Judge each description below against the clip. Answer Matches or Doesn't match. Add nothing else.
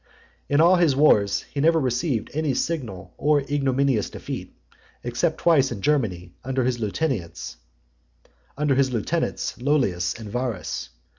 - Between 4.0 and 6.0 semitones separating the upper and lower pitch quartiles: Matches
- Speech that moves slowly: Matches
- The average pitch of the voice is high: Doesn't match